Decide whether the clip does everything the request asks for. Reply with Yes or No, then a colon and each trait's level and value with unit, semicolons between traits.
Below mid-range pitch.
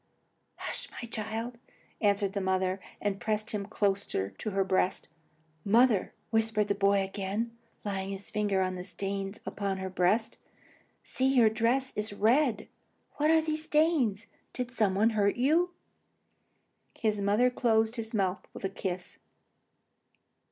No: high, 210 Hz